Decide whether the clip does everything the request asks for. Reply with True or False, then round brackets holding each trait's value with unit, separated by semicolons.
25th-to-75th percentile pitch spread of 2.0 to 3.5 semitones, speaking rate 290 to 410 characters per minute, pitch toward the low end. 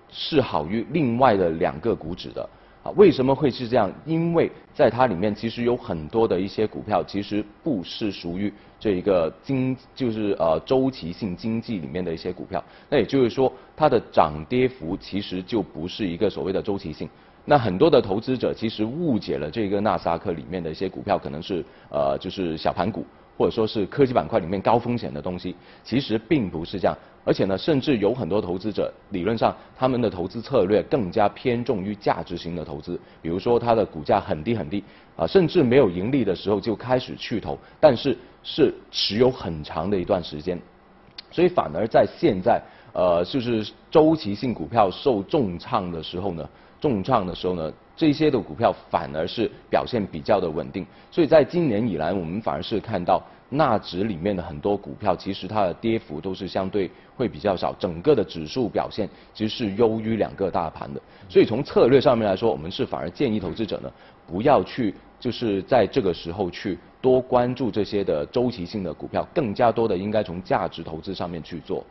False (5.2 semitones; 305 characters per minute; 105 Hz)